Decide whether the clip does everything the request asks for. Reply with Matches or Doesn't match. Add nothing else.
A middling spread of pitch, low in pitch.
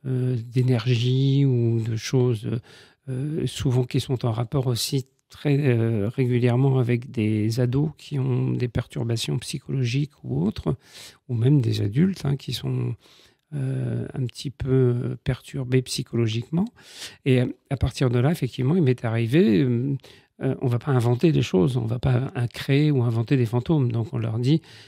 Doesn't match